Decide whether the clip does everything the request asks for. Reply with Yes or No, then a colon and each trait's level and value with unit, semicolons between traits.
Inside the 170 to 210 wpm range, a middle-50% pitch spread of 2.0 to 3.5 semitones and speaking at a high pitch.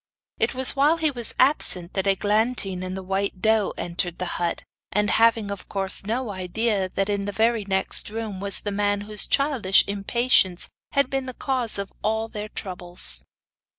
Yes: average, 180 wpm; average, 3.2 semitones; high, 205 Hz